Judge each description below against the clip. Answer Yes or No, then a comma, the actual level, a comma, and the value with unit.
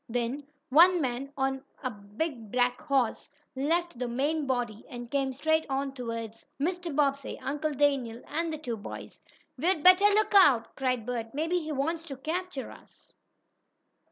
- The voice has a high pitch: Yes, very high, 275 Hz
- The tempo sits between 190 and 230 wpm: No, average, 155 wpm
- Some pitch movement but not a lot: Yes, average, 4.4 semitones